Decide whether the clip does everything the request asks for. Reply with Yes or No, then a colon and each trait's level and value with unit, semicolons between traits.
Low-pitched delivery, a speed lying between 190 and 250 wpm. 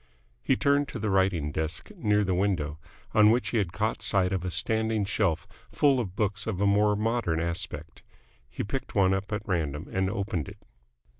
Yes: low, 100 Hz; average, 195 wpm